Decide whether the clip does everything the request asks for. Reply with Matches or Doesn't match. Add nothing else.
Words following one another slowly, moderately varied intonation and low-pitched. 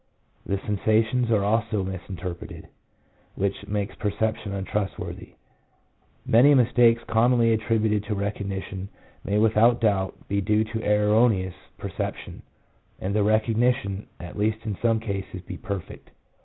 Doesn't match